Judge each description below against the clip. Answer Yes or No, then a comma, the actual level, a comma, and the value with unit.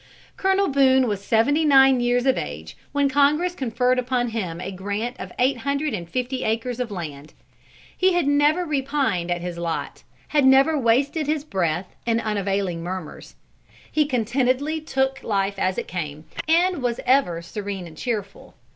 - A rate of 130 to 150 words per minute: No, average, 165 wpm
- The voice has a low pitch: No, high, 245 Hz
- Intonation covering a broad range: Yes, wide, 6.4 semitones